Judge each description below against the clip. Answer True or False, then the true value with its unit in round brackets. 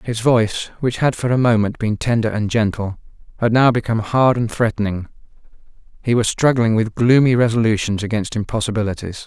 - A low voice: True (115 Hz)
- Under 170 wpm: True (160 wpm)